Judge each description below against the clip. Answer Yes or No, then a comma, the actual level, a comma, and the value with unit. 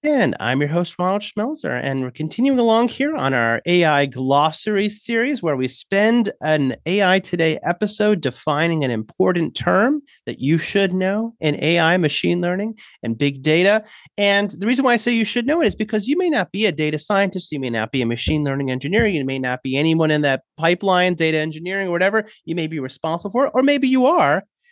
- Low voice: No, medium, 180 Hz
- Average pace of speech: No, fast, 210 wpm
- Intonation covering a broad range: Yes, wide, 6.2 semitones